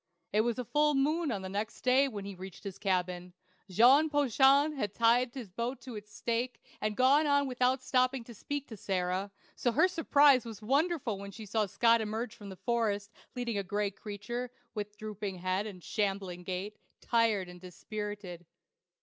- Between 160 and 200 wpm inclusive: Yes, average, 180 wpm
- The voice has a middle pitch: No, high, 220 Hz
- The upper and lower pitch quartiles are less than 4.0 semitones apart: No, average, 4.3 semitones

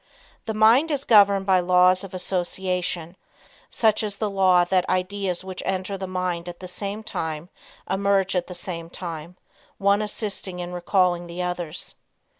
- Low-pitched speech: No, medium, 185 Hz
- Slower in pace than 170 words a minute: Yes, average, 160 wpm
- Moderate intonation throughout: No, narrow, 2.0 semitones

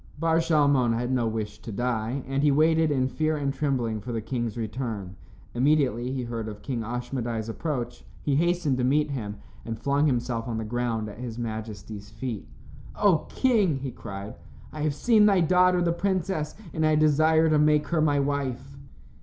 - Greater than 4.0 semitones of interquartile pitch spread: Yes, average, 4.9 semitones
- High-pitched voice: No, low, 130 Hz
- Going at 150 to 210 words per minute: Yes, average, 185 wpm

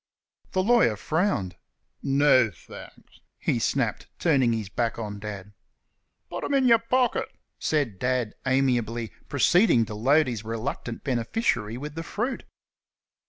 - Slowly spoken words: Yes, slow, 130 wpm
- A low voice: Yes, low, 125 Hz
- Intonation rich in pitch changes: Yes, wide, 6.4 semitones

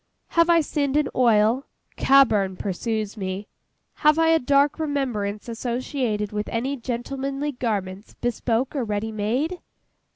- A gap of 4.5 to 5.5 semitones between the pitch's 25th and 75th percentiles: Yes, average, 4.9 semitones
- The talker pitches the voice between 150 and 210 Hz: No, high, 245 Hz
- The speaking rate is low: Yes, slow, 130 wpm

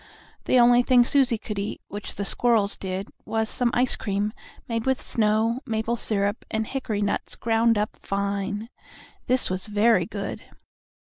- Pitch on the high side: Yes, high, 220 Hz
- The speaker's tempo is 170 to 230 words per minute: No, average, 160 wpm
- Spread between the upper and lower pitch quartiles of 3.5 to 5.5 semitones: No, average, 2.7 semitones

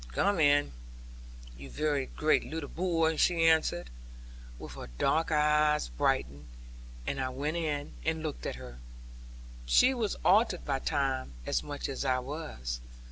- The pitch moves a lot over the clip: No, average, 3.8 semitones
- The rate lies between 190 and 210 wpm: No, average, 145 wpm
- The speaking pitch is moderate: Yes, medium, 150 Hz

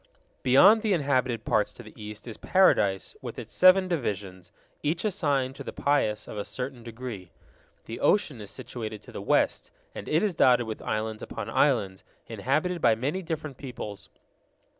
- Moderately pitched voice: No, low, 125 Hz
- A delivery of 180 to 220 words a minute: No, average, 170 wpm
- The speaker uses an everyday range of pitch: No, wide, 6.1 semitones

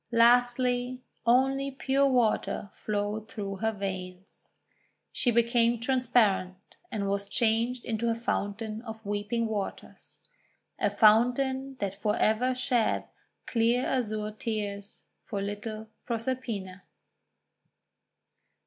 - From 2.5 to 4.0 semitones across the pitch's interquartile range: Yes, average, 3.2 semitones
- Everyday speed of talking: No, slow, 105 wpm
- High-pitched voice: Yes, high, 225 Hz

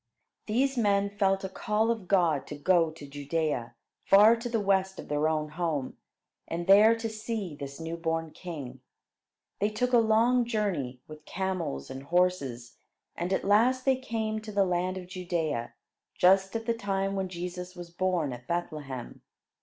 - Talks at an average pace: Yes, average, 170 wpm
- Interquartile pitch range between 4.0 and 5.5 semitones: Yes, average, 5.2 semitones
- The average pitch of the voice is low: No, medium, 185 Hz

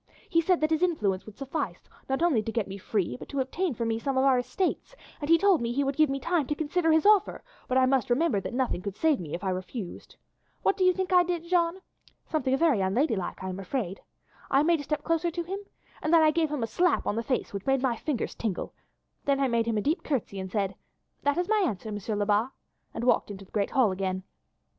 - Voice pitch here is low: No, very high, 270 Hz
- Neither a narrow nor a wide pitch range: No, wide, 7.5 semitones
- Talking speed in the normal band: No, fast, 255 wpm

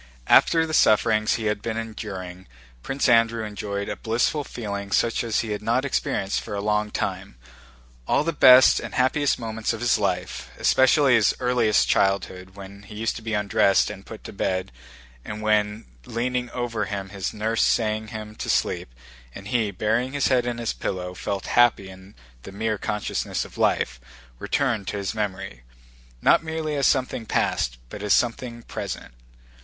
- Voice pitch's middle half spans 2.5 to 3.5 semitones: Yes, average, 3.1 semitones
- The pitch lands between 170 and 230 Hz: No, low, 110 Hz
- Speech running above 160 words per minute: Yes, average, 170 wpm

